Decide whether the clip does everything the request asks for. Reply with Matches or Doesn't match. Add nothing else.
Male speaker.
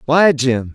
Matches